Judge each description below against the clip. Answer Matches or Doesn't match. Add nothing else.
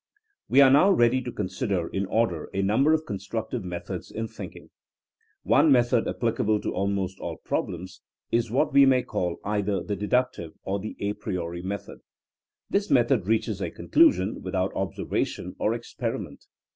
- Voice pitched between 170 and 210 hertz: Doesn't match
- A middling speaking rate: Matches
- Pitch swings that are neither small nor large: Matches